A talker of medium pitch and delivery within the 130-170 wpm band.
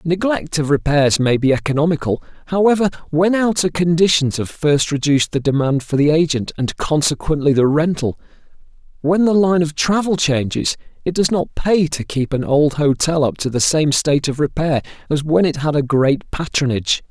No: medium, 150 Hz; average, 180 wpm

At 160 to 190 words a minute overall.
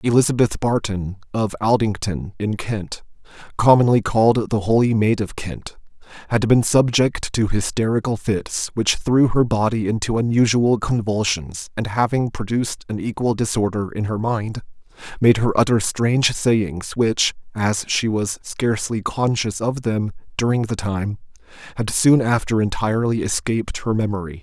No: average, 140 wpm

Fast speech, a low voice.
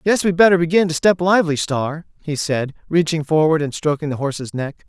No: fast, 210 wpm; medium, 160 Hz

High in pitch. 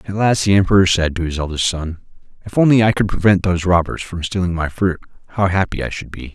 No: very low, 90 Hz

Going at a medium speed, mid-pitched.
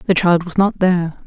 No: fast, 235 wpm; medium, 180 Hz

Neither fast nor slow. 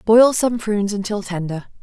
Yes: average, 165 wpm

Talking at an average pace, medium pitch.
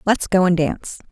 No: fast, 215 wpm; medium, 180 Hz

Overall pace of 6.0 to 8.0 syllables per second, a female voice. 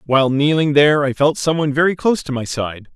No: 6.4 syllables/s; male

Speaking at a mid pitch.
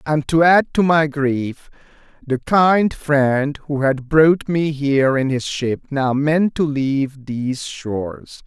Yes: medium, 145 Hz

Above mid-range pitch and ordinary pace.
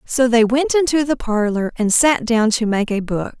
No: high, 240 Hz; fast, 230 wpm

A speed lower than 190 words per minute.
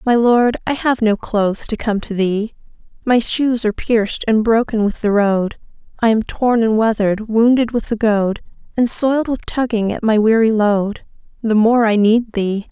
No: average, 195 wpm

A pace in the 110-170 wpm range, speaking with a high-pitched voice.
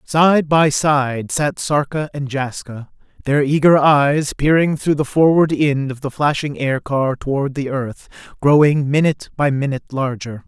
No: average, 155 wpm; medium, 140 Hz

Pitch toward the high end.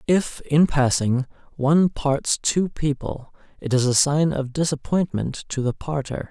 No: medium, 140 Hz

